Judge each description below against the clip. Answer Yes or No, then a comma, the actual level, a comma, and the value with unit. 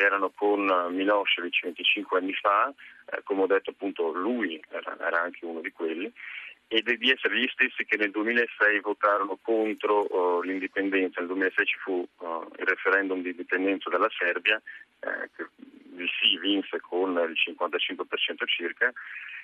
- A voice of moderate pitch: No, low, 100 Hz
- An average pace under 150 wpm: No, average, 155 wpm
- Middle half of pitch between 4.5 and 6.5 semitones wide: No, average, 3.2 semitones